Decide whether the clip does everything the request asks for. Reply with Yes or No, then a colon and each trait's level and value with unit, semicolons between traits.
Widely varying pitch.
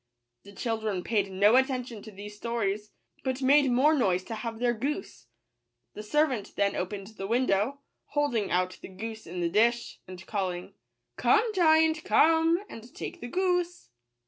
Yes: wide, 5.8 semitones